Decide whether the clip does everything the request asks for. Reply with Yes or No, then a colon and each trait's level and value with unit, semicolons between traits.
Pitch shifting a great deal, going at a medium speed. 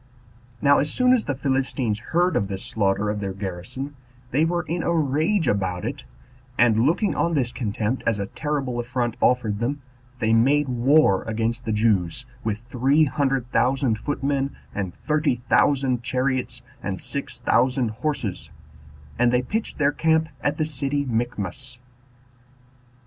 No: average, 4.5 semitones; average, 155 wpm